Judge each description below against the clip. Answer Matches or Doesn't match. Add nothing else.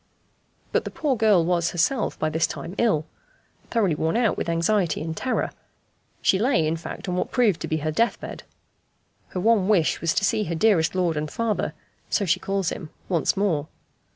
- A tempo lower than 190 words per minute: Doesn't match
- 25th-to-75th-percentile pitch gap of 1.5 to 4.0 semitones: Doesn't match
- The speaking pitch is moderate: Matches